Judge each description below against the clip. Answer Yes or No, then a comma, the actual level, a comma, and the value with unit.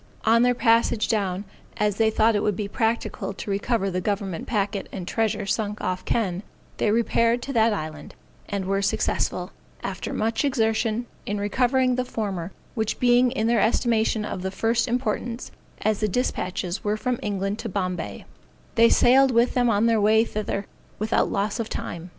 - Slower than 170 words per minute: No, average, 175 wpm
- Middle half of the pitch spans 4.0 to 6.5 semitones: No, average, 2.7 semitones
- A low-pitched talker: No, high, 215 Hz